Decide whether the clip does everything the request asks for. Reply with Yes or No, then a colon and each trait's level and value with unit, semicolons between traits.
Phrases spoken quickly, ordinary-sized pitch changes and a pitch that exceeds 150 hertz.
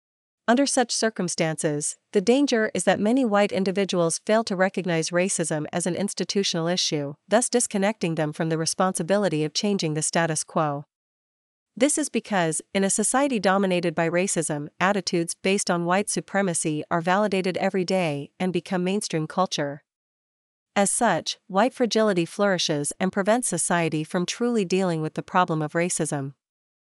No: average, 150 wpm; average, 3.8 semitones; medium, 185 Hz